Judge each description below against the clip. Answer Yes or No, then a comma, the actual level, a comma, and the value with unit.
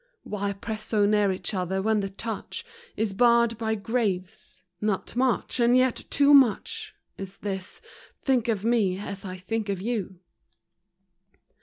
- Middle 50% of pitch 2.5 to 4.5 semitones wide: Yes, average, 3.2 semitones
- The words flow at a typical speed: Yes, average, 155 wpm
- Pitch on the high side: Yes, high, 215 Hz